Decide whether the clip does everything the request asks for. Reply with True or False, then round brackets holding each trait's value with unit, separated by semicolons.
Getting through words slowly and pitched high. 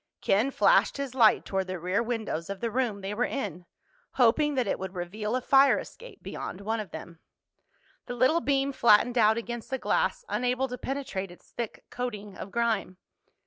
False (185 wpm; 230 Hz)